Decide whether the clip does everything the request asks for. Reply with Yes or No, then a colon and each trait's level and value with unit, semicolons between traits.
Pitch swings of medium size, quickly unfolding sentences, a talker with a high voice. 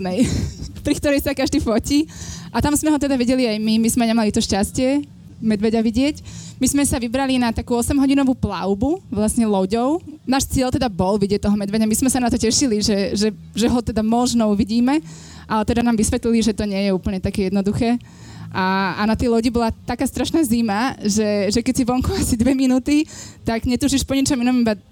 Yes: average, 3.7 semitones; fast, 200 wpm; high, 235 Hz